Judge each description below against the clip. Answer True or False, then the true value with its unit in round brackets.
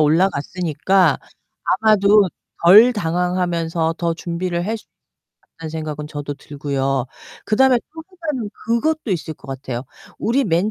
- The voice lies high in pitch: False (175 Hz)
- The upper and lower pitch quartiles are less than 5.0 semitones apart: False (5.6 semitones)